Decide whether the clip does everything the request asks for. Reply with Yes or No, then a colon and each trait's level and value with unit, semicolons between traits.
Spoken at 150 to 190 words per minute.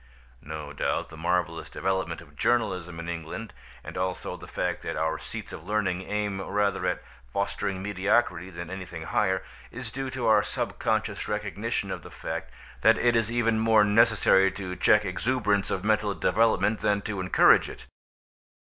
Yes: average, 165 wpm